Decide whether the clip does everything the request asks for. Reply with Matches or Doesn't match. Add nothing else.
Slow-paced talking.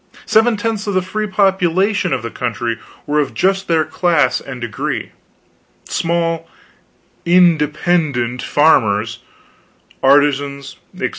Matches